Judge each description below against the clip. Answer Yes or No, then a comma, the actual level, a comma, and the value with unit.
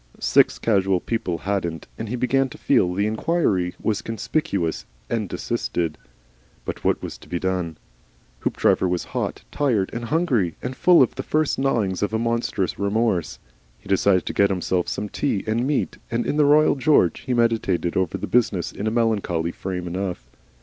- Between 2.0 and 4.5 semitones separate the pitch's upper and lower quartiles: No, average, 4.9 semitones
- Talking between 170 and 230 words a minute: Yes, average, 175 wpm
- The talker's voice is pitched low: Yes, low, 105 Hz